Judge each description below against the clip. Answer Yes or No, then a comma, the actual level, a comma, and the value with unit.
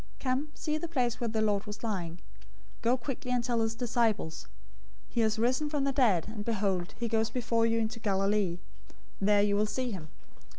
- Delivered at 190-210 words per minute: Yes, average, 200 wpm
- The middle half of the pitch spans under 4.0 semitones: Yes, average, 3.2 semitones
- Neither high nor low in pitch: No, high, 225 Hz